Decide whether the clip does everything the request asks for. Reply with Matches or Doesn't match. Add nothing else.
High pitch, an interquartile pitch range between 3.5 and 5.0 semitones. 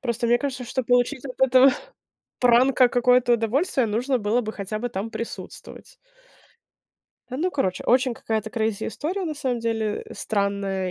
Doesn't match